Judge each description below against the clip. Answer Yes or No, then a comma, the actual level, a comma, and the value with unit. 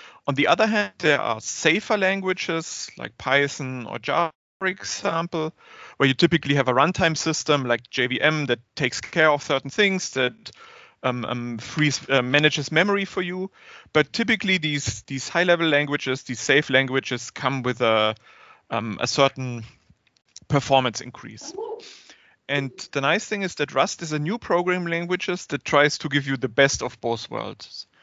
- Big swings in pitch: No, average, 5.0 semitones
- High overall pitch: No, medium, 145 Hz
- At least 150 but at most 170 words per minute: Yes, average, 165 wpm